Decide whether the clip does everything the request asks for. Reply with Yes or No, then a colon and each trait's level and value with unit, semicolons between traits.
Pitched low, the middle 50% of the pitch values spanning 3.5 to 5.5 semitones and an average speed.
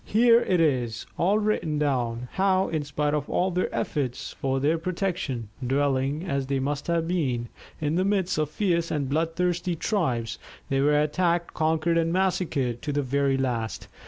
No: medium, 150 Hz; average, 4.5 semitones; average, 170 wpm